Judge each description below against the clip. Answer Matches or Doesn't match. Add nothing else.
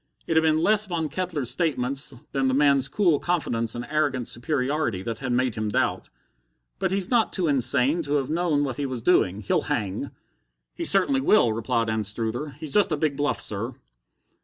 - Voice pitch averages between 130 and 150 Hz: Matches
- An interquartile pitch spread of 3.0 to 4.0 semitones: Doesn't match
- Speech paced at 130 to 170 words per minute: Doesn't match